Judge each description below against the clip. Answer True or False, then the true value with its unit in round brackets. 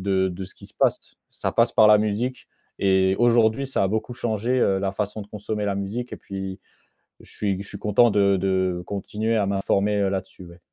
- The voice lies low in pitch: True (100 Hz)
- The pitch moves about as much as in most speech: False (2.1 semitones)